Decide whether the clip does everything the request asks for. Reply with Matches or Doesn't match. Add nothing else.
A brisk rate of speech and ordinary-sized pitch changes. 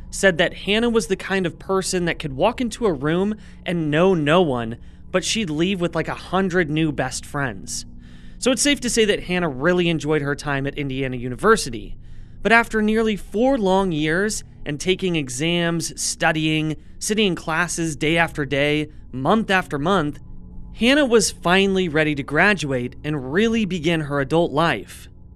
Doesn't match